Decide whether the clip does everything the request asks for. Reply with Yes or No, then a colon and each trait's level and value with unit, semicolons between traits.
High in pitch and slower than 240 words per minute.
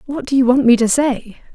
No: very high, 250 Hz; fast, 275 wpm